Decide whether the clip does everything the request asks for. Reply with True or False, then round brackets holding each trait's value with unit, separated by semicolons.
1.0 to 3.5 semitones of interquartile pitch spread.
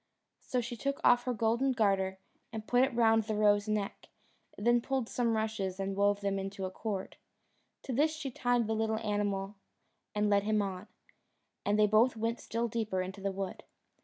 True (2.9 semitones)